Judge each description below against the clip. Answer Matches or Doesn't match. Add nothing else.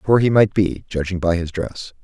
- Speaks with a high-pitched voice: Doesn't match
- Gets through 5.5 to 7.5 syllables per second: Doesn't match